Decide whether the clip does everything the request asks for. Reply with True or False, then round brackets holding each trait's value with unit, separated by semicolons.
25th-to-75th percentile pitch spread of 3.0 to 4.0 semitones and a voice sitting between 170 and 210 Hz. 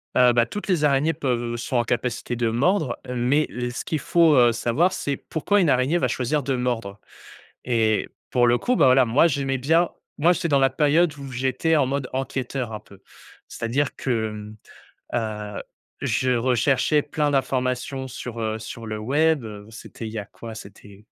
False (3.7 semitones; 125 Hz)